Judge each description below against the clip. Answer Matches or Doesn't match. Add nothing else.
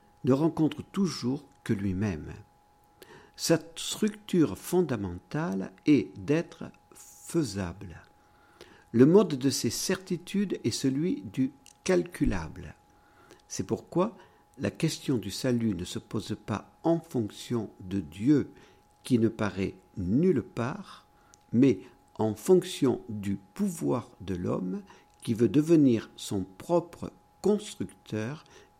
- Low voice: Matches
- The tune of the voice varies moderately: Doesn't match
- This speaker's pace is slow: Matches